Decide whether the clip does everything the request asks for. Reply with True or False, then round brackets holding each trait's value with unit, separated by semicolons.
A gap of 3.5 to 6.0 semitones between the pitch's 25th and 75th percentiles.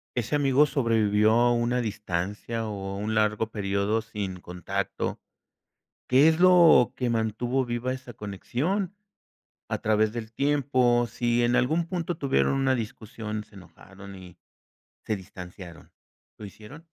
True (3.9 semitones)